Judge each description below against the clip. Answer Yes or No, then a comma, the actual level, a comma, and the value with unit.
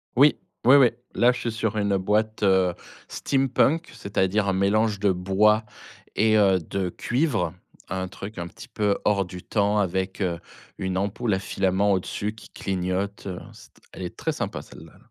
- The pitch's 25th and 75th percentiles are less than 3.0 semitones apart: Yes, narrow, 2.5 semitones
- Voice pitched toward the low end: Yes, low, 100 Hz